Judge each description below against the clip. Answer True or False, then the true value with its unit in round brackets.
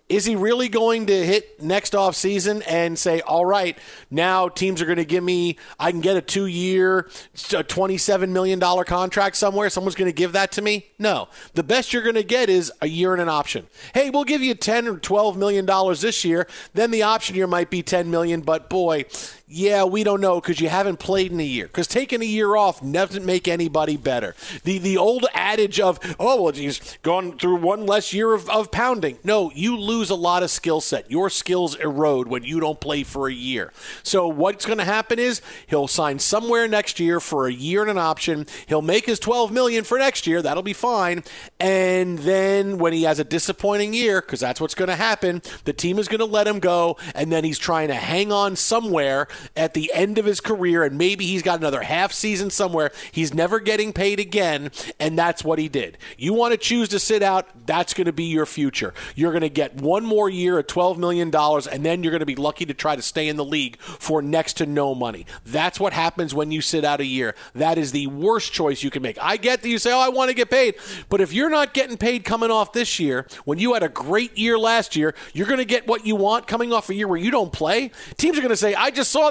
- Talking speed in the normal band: False (240 wpm)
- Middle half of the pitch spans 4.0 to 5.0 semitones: True (4.6 semitones)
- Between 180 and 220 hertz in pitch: True (185 Hz)